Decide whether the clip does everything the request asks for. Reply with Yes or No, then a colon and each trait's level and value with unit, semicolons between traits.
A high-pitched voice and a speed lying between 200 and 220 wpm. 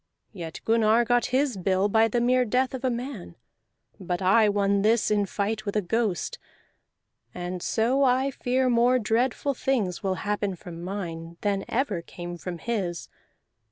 No: high, 215 Hz; average, 160 wpm